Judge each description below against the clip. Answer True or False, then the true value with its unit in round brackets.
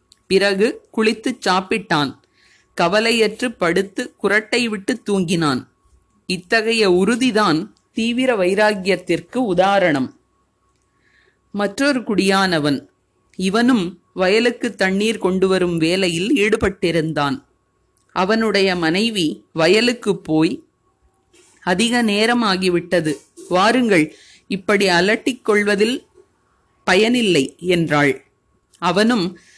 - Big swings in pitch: False (4.7 semitones)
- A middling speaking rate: False (70 wpm)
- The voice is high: True (200 Hz)